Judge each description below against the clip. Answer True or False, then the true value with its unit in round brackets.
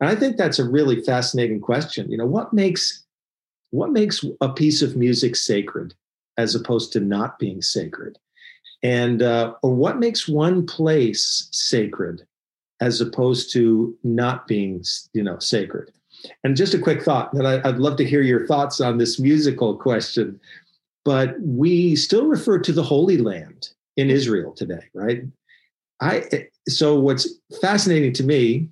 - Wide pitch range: False (4.5 semitones)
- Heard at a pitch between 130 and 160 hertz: True (135 Hz)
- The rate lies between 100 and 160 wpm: True (155 wpm)